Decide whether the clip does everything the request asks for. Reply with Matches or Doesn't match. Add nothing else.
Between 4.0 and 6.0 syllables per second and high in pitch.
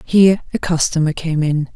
Doesn't match